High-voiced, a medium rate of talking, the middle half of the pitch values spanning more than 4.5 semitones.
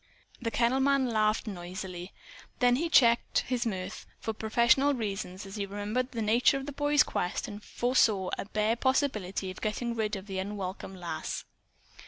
No: high, 215 Hz; average, 170 wpm; average, 4.1 semitones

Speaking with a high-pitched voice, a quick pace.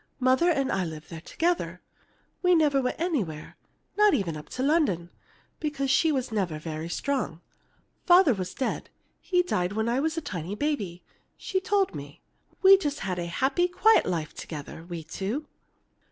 No: very high, 255 Hz; average, 170 wpm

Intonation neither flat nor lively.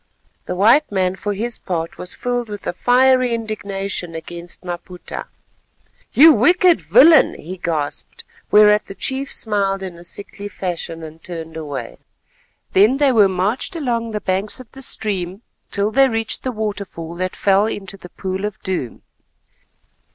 Yes: average, 4.4 semitones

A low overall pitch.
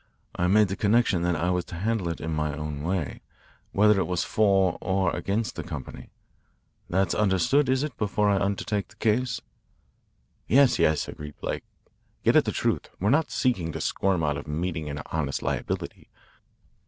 Yes: very low, 95 Hz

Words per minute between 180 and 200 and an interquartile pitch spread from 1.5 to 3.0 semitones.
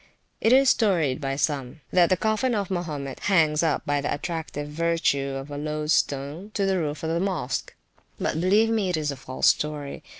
No: average, 195 wpm; average, 4.4 semitones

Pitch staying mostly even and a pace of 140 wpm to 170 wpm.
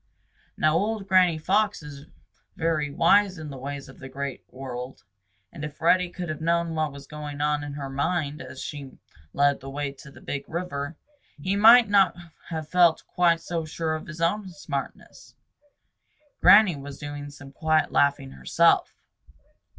No: average, 3.5 semitones; average, 165 wpm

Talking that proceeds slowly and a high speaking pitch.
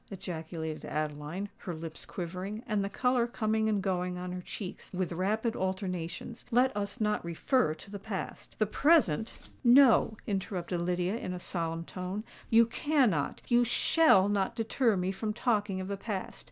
No: average, 165 wpm; high, 195 Hz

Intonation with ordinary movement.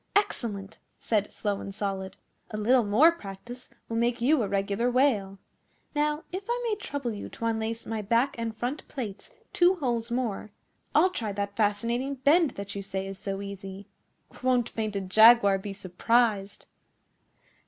Yes: average, 4.1 semitones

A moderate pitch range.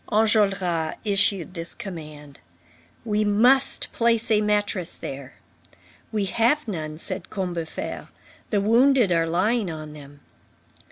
Yes: average, 4.7 semitones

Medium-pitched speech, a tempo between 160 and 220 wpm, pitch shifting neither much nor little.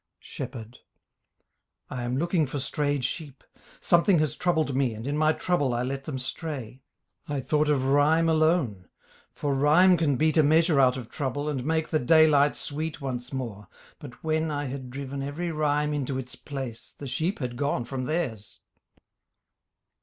Yes: medium, 145 Hz; average, 170 wpm; average, 3.3 semitones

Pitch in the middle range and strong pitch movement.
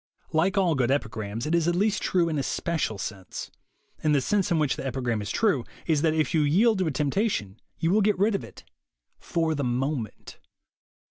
Yes: medium, 155 Hz; wide, 6.0 semitones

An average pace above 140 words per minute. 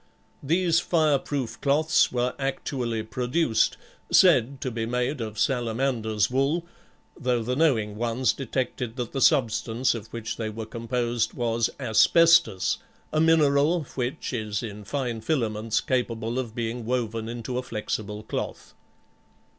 No: slow, 135 wpm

